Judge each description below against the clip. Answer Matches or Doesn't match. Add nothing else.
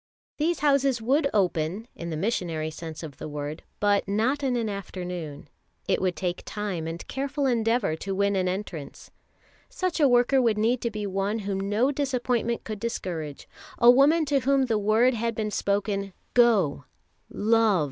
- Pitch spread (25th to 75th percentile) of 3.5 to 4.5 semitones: Doesn't match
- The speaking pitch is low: Doesn't match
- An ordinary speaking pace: Matches